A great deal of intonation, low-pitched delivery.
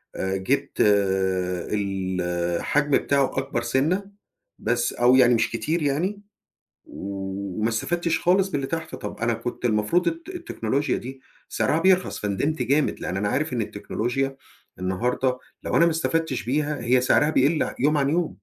Yes: wide, 7.0 semitones; low, 130 Hz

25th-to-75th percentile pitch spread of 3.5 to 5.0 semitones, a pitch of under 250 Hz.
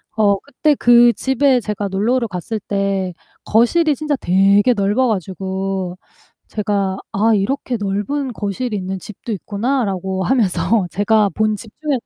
Yes: average, 4.0 semitones; high, 210 Hz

